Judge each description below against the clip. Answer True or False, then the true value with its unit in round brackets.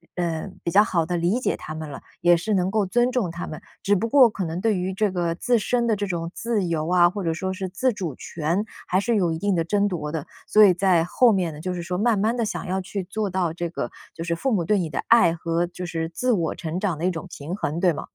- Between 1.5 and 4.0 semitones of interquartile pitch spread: True (3.5 semitones)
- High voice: False (180 Hz)